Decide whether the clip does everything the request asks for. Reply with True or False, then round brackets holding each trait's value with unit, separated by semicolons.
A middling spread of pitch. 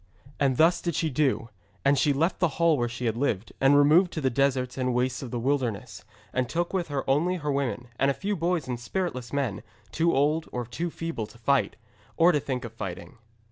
True (4.8 semitones)